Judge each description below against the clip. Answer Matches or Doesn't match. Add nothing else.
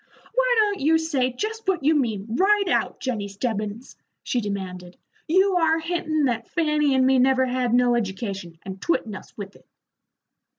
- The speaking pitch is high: Matches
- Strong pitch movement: Matches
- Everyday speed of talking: Matches